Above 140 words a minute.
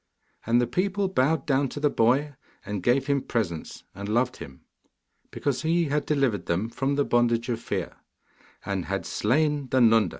Yes: average, 175 wpm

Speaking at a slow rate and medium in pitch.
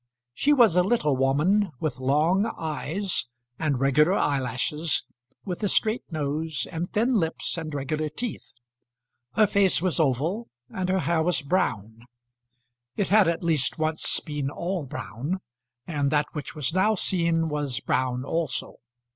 No: average, 145 wpm; medium, 160 Hz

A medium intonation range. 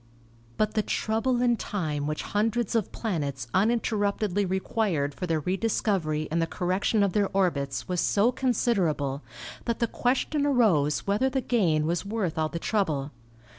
No: wide, 6.2 semitones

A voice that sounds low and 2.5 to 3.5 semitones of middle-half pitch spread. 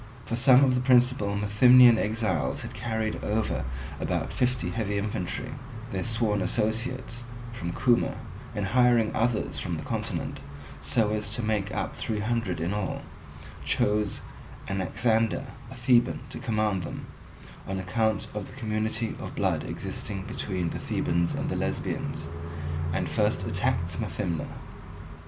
Yes: low, 110 Hz; average, 3.1 semitones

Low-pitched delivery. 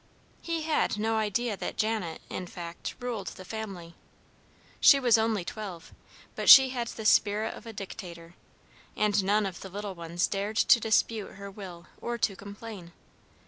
No: high, 205 Hz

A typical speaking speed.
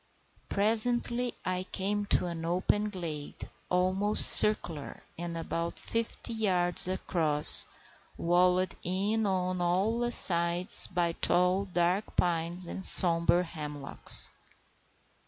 No: slow, 100 wpm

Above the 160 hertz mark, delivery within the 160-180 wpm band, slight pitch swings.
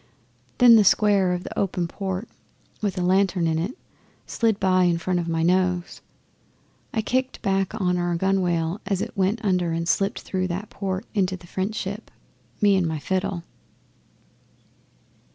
Yes: medium, 185 Hz; average, 165 wpm; narrow, 2.2 semitones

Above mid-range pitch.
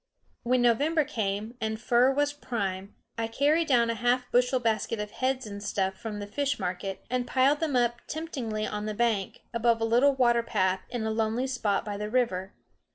Yes: high, 235 Hz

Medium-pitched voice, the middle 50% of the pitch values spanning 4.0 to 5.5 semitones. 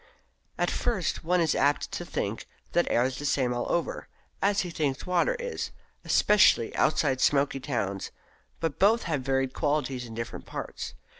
Yes: medium, 145 Hz; average, 5.2 semitones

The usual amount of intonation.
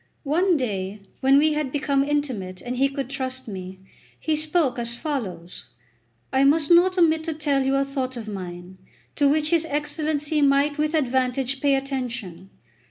Yes: average, 3.7 semitones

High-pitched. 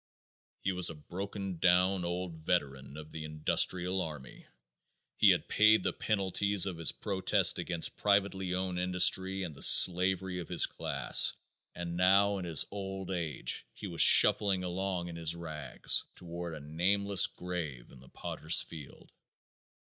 No: very low, 90 Hz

